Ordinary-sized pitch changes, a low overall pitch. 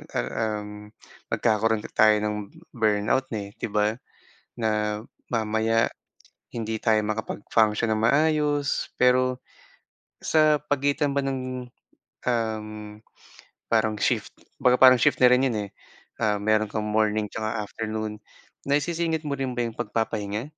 Yes: average, 3.1 semitones; low, 110 Hz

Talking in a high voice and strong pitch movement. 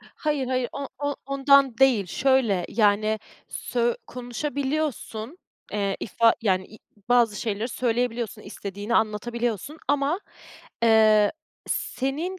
No: high, 240 Hz; average, 4.2 semitones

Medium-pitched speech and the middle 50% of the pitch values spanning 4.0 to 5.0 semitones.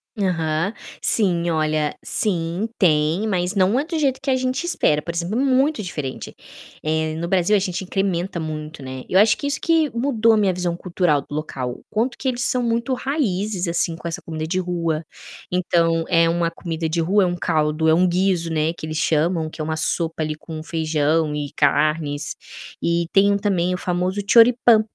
Yes: medium, 175 Hz; average, 4.6 semitones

